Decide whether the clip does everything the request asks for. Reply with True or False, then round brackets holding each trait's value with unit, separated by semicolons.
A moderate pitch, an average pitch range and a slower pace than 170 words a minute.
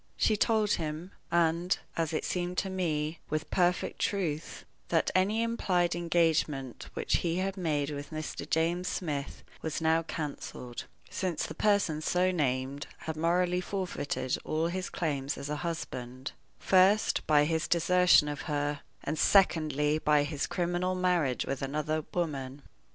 True (160 Hz; 3.4 semitones; 145 wpm)